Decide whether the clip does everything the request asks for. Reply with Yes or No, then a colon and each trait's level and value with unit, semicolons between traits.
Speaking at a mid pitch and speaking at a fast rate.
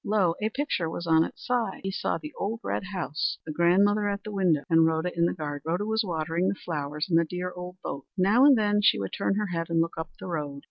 Yes: medium, 180 Hz; fast, 260 wpm